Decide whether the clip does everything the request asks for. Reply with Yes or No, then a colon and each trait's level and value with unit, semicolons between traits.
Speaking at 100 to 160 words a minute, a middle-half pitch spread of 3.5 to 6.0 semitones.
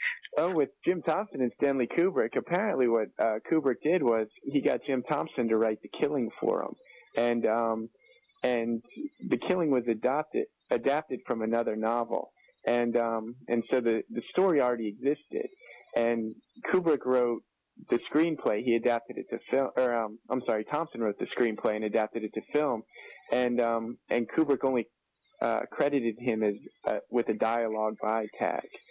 No: average, 170 wpm; average, 4.0 semitones